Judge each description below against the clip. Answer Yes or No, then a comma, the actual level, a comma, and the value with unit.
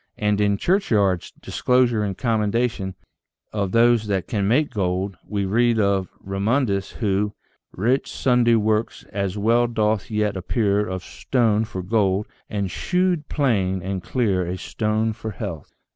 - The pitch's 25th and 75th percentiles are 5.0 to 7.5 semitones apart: No, average, 3.2 semitones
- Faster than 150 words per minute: No, average, 145 wpm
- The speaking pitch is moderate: No, low, 105 Hz